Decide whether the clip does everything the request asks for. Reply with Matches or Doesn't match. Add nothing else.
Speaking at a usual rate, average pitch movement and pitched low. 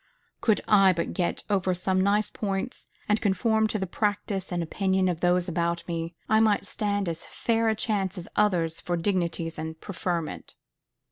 Doesn't match